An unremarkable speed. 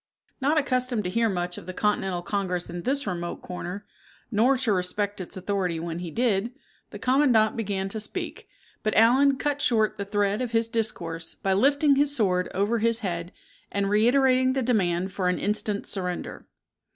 Yes: average, 175 wpm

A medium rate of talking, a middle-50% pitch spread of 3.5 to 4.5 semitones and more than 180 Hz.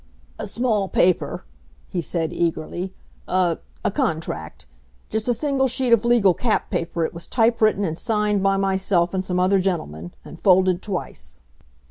Yes: average, 160 wpm; average, 4.0 semitones; high, 190 Hz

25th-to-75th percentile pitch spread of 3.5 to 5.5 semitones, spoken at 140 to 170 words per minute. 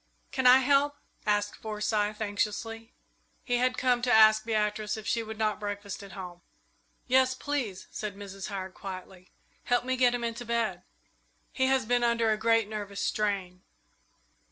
No: average, 3.1 semitones; average, 160 wpm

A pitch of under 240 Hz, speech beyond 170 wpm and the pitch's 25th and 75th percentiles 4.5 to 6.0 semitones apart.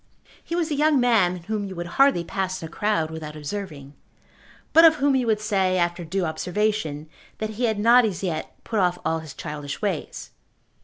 Yes: high, 190 Hz; average, 200 wpm; average, 5.2 semitones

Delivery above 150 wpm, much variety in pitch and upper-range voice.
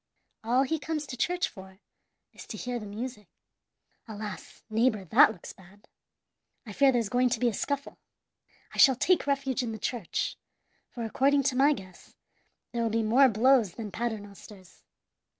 No: average, 170 wpm; average, 4.3 semitones; high, 235 Hz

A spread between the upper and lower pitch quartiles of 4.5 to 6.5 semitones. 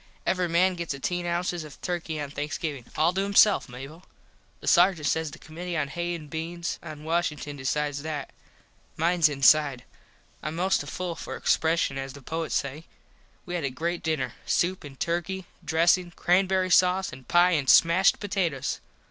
No: average, 3.2 semitones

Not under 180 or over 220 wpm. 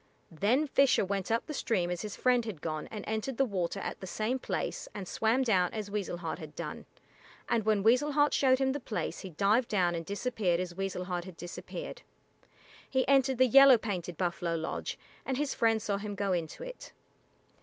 Yes: fast, 205 wpm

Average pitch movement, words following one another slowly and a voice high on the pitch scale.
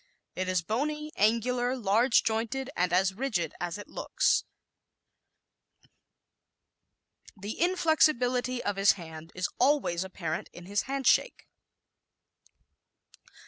No: wide, 6.1 semitones; slow, 100 wpm; high, 220 Hz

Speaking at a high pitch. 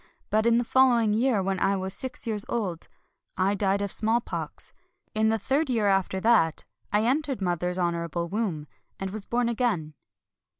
Yes: high, 210 Hz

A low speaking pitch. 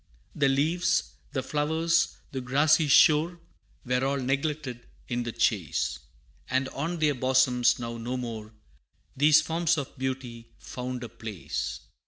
Yes: low, 130 Hz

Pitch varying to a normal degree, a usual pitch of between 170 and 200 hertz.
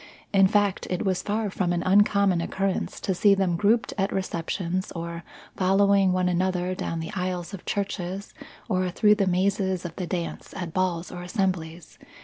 No: narrow, 1.8 semitones; medium, 185 Hz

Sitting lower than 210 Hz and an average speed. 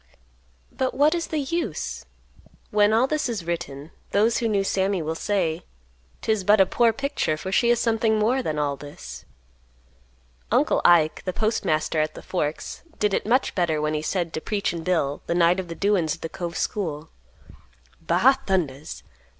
Yes: high, 190 Hz; average, 175 wpm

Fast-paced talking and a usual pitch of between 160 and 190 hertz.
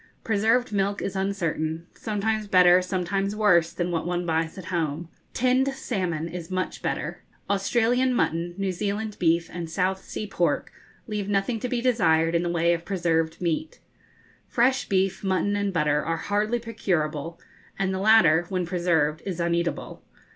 No: average, 160 wpm; medium, 185 Hz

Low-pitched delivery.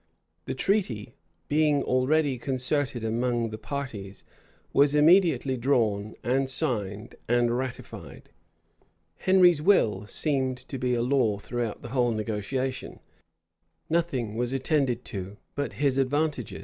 Yes: low, 130 Hz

